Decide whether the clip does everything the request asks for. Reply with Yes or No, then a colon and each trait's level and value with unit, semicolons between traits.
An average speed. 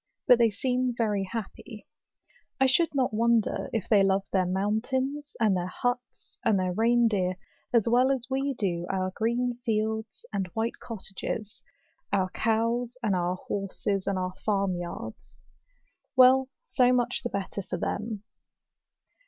Yes: average, 150 wpm